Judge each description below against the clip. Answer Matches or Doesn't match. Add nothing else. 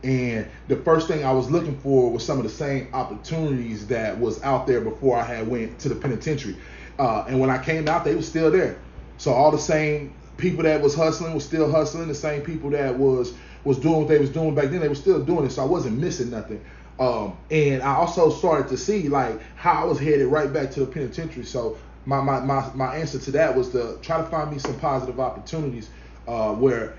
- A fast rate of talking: Matches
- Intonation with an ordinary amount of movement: Matches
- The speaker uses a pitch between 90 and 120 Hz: Doesn't match